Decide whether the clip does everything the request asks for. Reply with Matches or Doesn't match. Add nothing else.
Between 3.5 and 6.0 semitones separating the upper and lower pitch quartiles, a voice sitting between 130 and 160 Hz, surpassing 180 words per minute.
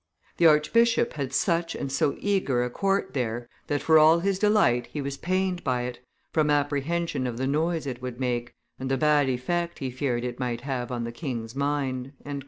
Matches